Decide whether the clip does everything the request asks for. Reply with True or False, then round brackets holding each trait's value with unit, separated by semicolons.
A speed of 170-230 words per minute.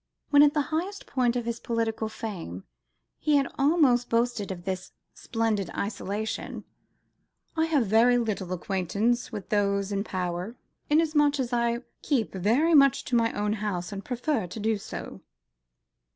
False (150 wpm)